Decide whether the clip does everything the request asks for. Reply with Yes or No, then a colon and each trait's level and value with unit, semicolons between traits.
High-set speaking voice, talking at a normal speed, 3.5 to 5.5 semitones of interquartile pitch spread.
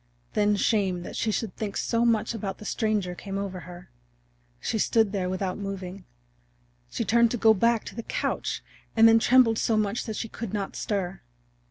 No: high, 210 Hz; average, 190 wpm; average, 2.7 semitones